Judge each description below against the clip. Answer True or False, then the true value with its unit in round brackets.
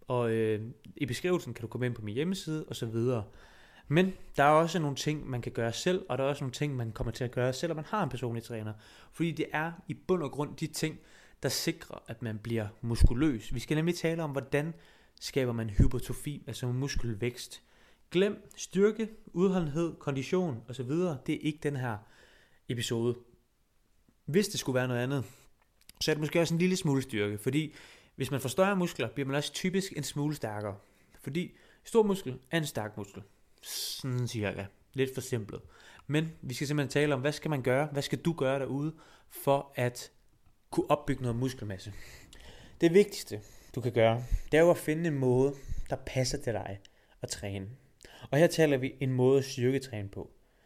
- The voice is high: False (135 Hz)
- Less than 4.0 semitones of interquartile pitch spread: False (4.6 semitones)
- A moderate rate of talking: True (200 wpm)